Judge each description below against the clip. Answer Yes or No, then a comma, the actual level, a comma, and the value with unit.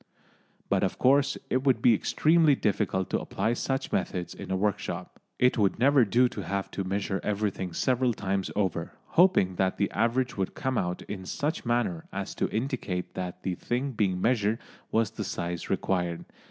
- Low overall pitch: Yes, low, 105 Hz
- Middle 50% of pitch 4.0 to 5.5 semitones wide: Yes, average, 4.9 semitones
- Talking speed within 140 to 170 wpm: No, average, 180 wpm